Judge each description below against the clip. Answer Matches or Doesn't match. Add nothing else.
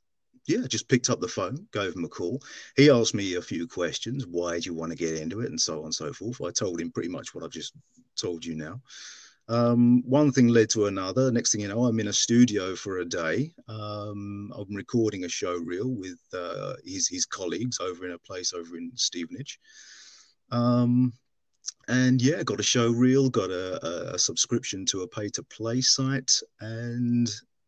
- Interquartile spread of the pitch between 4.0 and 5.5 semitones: Matches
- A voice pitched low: Matches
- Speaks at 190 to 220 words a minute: Matches